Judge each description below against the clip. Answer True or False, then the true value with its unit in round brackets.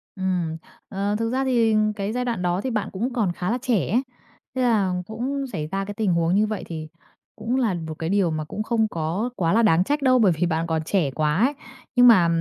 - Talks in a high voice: True (200 Hz)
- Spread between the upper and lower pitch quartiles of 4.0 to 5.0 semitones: False (5.6 semitones)